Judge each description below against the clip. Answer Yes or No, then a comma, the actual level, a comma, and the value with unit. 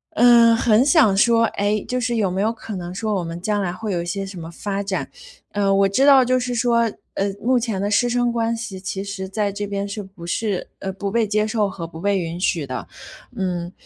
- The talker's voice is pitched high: Yes, high, 205 Hz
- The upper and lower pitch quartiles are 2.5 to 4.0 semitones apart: Yes, average, 3.2 semitones